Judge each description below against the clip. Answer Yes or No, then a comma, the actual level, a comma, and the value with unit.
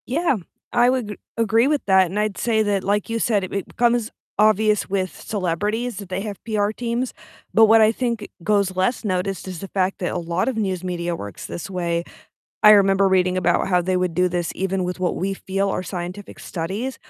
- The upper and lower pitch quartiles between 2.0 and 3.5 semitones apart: Yes, average, 3.1 semitones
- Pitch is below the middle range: No, high, 195 Hz